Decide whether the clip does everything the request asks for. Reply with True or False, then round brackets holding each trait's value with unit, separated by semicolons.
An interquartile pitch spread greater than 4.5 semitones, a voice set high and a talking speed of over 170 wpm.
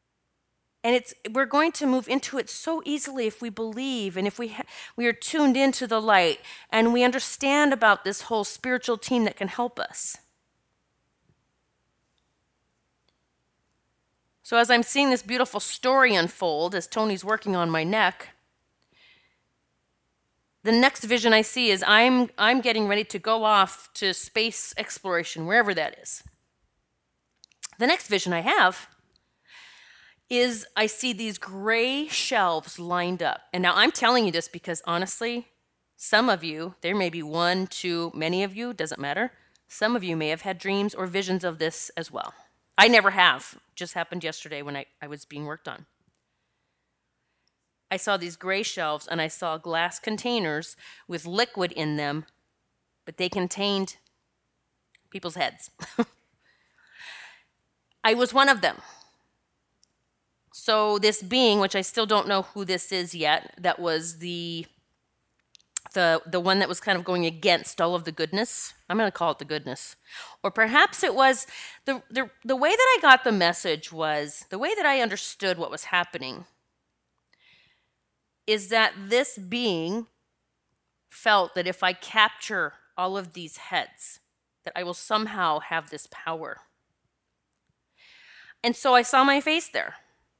False (5.6 semitones; 200 Hz; 155 wpm)